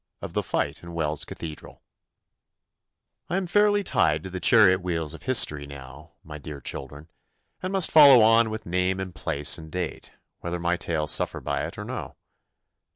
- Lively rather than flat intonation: Yes, wide, 6.3 semitones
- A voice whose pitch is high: No, very low, 85 Hz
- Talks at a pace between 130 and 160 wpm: No, average, 175 wpm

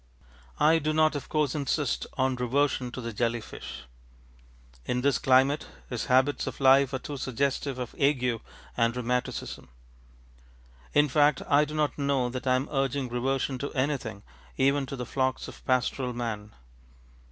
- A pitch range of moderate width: No, narrow, 2.3 semitones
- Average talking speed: Yes, average, 160 wpm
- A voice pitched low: Yes, low, 130 Hz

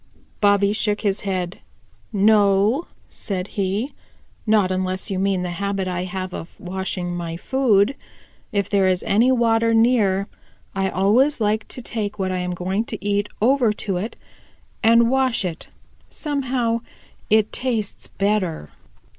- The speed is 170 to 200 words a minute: No, average, 145 wpm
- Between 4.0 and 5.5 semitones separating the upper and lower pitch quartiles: No, average, 3.3 semitones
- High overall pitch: Yes, high, 200 Hz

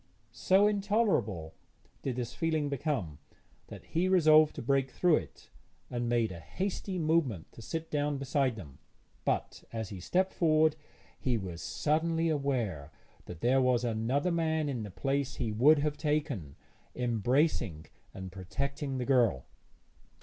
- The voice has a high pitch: No, low, 135 Hz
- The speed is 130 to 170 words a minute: Yes, average, 145 wpm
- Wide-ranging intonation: Yes, wide, 5.9 semitones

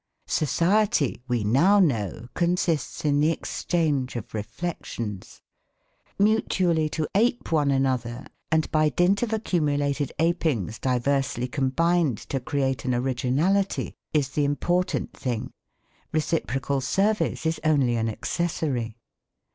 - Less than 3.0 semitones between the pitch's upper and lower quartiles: No, average, 5.2 semitones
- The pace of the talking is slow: Yes, slow, 115 wpm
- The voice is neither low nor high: Yes, medium, 145 Hz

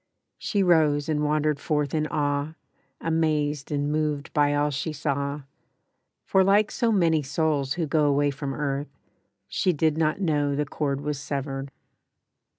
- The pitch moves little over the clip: Yes, narrow, 1.7 semitones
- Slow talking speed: No, average, 155 wpm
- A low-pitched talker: No, medium, 150 Hz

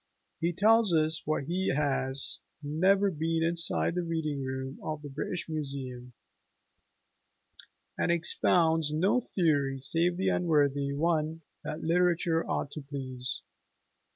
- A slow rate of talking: Yes, slow, 125 wpm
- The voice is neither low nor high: Yes, medium, 155 Hz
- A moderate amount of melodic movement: Yes, average, 3.3 semitones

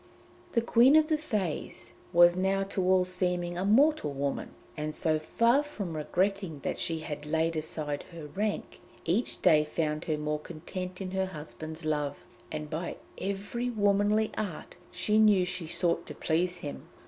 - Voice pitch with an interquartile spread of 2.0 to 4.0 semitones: No, average, 4.5 semitones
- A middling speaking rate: Yes, average, 165 wpm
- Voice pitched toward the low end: No, medium, 180 Hz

